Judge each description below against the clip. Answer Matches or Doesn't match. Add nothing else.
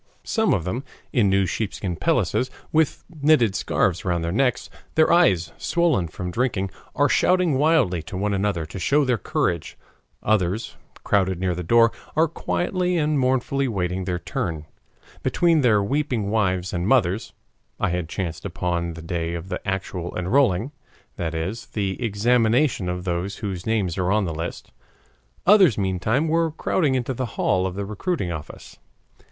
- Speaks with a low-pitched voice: Matches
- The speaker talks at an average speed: Matches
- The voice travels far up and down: Matches